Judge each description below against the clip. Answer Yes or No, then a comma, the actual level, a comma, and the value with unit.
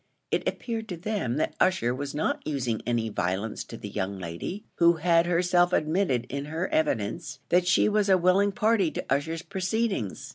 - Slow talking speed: No, average, 180 wpm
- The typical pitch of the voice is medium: Yes, medium, 165 Hz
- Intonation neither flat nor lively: No, wide, 7.5 semitones